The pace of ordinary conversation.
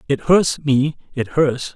Yes: average, 170 wpm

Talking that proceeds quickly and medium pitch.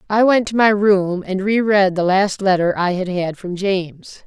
No: fast, 225 wpm; high, 195 Hz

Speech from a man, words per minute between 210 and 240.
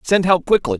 Yes: male; fast, 230 wpm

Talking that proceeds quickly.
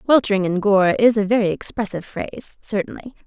No: average, 165 wpm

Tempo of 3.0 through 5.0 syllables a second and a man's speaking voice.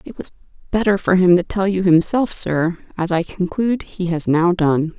No: 4.9 syllables/s; female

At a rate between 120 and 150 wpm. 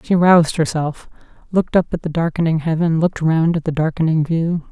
No: average, 190 wpm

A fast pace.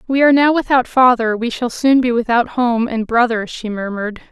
Yes: fast, 210 wpm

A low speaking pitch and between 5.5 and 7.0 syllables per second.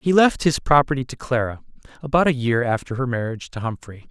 Yes: low, 130 Hz; 6.0 syllables/s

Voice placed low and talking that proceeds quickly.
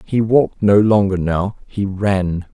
No: low, 100 Hz; average, 160 wpm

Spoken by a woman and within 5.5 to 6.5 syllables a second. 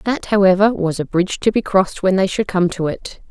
Yes: female; 5.6 syllables/s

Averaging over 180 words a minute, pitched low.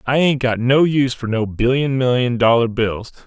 Yes: average, 200 wpm; low, 125 Hz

